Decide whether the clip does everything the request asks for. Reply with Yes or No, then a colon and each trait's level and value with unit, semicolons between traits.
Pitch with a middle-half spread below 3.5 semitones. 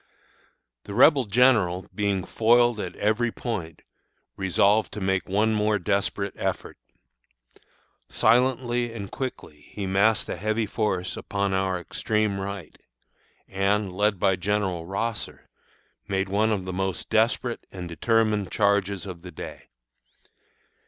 Yes: narrow, 2.5 semitones